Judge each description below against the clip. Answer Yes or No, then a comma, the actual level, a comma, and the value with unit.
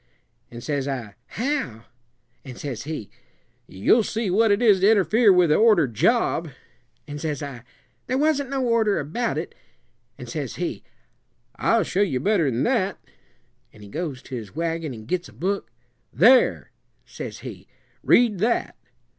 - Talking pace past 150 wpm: Yes, average, 160 wpm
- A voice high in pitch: No, medium, 180 Hz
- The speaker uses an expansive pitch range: Yes, wide, 8.9 semitones